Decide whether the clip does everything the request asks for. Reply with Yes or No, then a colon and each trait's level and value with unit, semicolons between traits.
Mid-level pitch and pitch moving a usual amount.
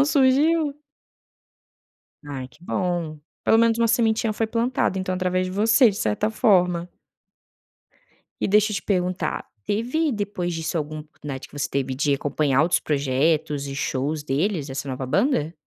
No: medium, 180 Hz; wide, 7.0 semitones